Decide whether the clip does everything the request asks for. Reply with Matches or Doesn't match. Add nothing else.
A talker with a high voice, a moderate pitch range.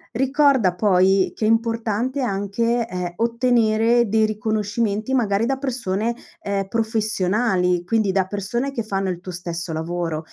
Matches